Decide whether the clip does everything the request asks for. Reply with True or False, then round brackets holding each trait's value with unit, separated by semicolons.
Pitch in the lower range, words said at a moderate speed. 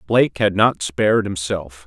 True (95 Hz; 160 wpm)